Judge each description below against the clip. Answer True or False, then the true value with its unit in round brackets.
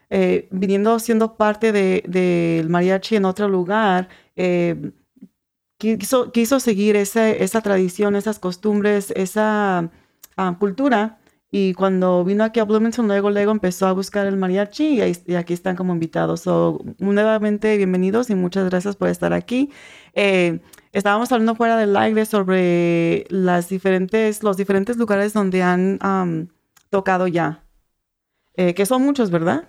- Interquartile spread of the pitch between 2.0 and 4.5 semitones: True (2.9 semitones)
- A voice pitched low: False (195 Hz)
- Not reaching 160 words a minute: True (150 wpm)